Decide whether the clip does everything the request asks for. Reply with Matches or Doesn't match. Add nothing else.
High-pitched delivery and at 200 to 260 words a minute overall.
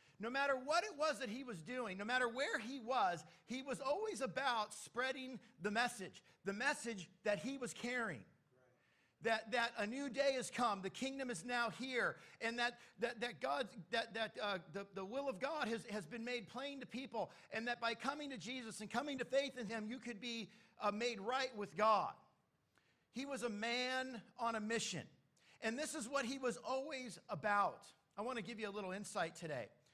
Matches